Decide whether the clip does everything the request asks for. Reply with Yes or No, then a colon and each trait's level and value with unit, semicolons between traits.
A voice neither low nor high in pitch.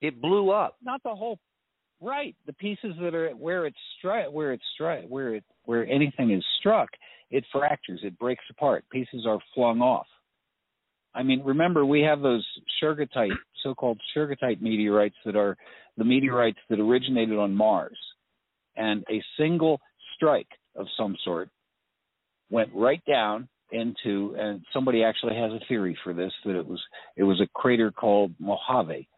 No: low, 125 Hz